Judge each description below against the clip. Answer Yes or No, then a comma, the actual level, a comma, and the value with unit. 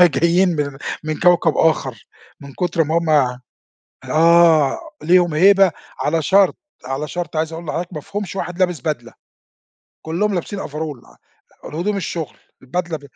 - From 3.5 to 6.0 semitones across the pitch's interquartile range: No, average, 2.8 semitones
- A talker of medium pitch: Yes, medium, 165 Hz